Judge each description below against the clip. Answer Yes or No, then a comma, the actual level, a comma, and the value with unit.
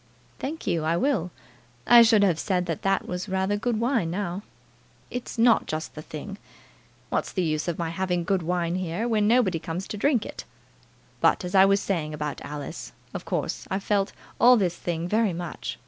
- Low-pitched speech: No, medium, 185 Hz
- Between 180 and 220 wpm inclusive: Yes, average, 195 wpm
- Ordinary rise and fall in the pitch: Yes, average, 3.9 semitones